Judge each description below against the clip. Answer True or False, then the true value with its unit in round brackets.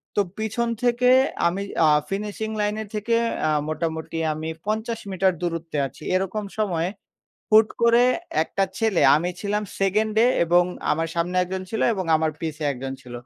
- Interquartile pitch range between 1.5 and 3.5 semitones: False (4.7 semitones)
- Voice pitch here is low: False (190 Hz)